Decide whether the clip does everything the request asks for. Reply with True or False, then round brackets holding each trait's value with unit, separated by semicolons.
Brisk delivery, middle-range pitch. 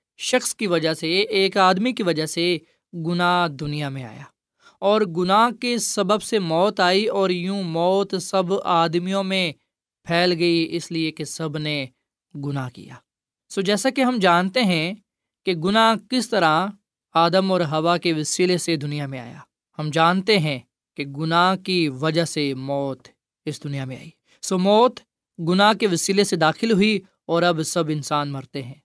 False (170 wpm; 175 Hz)